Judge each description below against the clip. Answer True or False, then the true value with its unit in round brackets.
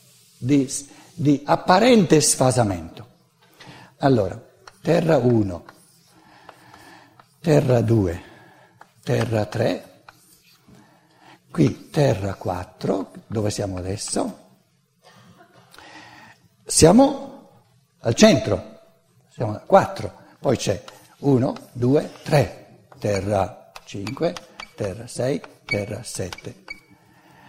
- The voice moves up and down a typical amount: False (7.1 semitones)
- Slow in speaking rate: True (75 wpm)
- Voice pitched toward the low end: True (125 Hz)